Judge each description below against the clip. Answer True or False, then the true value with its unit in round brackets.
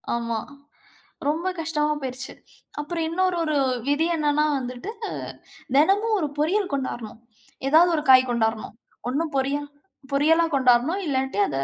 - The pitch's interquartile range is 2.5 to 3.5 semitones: False (4.1 semitones)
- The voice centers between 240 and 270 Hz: False (290 Hz)